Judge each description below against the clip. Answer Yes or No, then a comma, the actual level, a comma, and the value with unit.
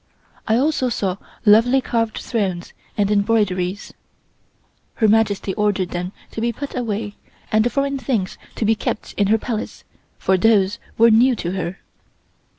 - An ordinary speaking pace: Yes, average, 155 wpm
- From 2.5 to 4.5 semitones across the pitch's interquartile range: Yes, average, 2.9 semitones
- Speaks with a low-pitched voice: No, high, 215 Hz